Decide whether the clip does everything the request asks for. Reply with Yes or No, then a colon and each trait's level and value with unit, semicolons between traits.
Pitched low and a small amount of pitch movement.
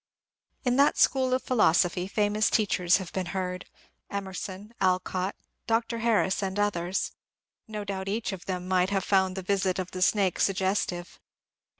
No: high, 190 Hz; narrow, 2.2 semitones